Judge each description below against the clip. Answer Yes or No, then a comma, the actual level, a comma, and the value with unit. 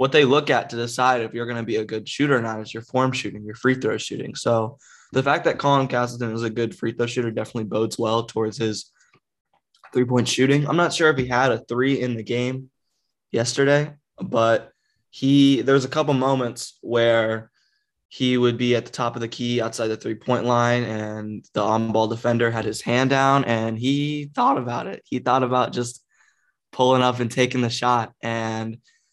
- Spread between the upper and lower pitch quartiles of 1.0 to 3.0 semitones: Yes, narrow, 2.4 semitones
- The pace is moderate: No, fast, 210 wpm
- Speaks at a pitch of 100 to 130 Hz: Yes, low, 120 Hz